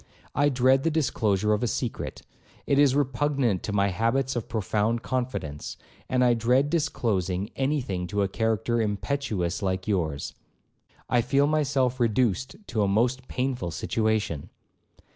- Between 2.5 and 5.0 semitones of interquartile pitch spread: Yes, average, 4.6 semitones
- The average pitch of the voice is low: Yes, low, 120 Hz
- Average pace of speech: Yes, average, 145 wpm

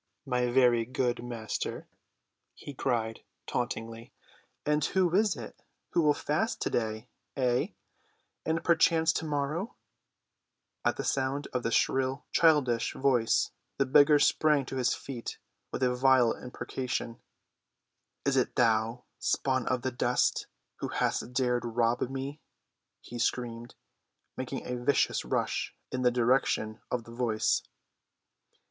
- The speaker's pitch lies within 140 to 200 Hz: No, low, 125 Hz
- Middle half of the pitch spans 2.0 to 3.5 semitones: Yes, average, 2.7 semitones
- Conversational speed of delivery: No, slow, 125 wpm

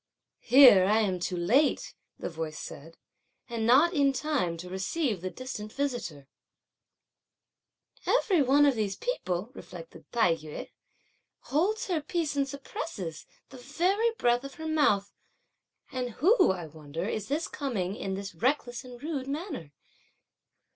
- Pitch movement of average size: No, wide, 7.6 semitones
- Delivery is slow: No, average, 145 wpm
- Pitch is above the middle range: Yes, high, 245 Hz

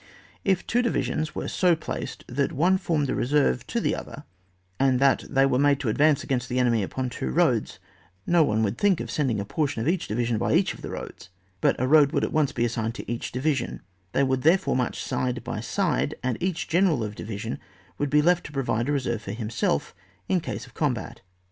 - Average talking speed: No, fast, 225 wpm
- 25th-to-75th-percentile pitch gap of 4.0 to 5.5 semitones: Yes, average, 4.8 semitones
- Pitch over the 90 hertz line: Yes, low, 135 Hz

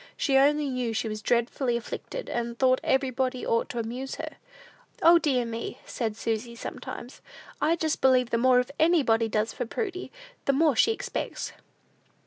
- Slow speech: No, average, 160 wpm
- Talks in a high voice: Yes, very high, 255 Hz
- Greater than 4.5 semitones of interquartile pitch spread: No, average, 3.3 semitones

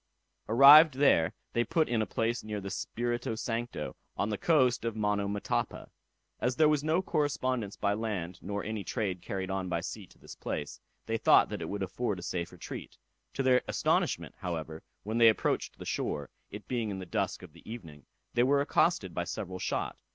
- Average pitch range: Yes, average, 4.6 semitones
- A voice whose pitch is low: Yes, low, 105 Hz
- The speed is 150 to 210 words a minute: Yes, average, 195 wpm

